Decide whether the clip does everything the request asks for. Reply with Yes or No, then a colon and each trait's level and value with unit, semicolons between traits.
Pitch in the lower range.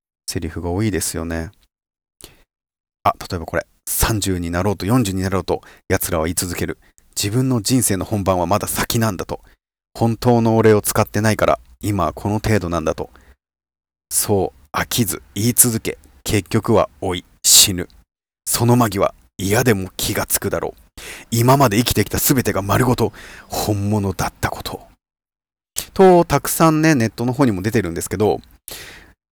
Yes: low, 100 Hz